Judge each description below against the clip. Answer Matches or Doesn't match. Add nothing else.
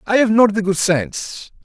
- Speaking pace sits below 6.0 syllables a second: Matches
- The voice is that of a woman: Doesn't match